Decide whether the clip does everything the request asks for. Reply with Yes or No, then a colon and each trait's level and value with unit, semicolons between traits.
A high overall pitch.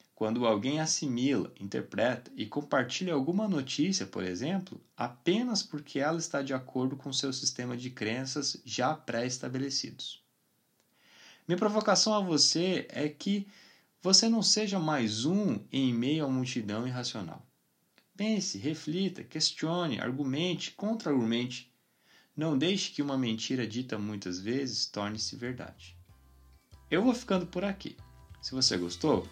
No: medium, 140 Hz